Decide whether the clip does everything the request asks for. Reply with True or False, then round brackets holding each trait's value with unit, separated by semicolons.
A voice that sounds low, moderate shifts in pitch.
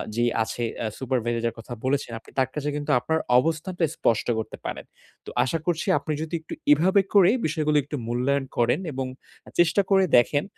False (145 Hz; 5.0 semitones)